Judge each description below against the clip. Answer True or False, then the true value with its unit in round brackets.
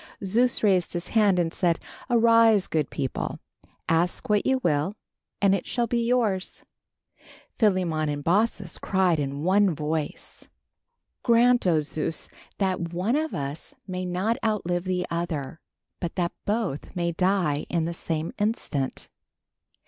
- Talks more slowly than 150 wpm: True (140 wpm)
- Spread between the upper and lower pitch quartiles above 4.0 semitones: True (4.5 semitones)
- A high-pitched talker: False (180 Hz)